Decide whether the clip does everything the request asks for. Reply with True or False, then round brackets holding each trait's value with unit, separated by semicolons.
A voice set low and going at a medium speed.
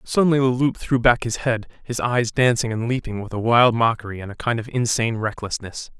False (115 Hz; 220 wpm)